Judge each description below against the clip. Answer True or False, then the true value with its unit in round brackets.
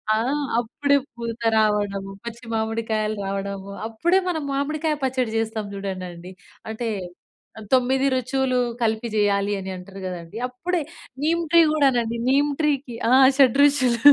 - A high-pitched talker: True (235 Hz)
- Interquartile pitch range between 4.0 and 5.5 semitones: True (4.7 semitones)